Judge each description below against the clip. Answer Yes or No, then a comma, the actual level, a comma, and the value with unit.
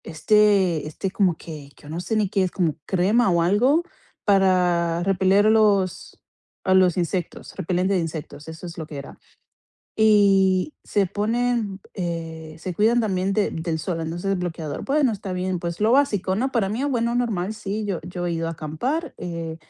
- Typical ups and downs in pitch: Yes, average, 3.9 semitones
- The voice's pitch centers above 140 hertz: Yes, medium, 185 Hz